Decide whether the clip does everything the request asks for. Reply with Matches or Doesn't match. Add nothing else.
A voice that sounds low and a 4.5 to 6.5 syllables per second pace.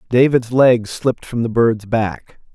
Doesn't match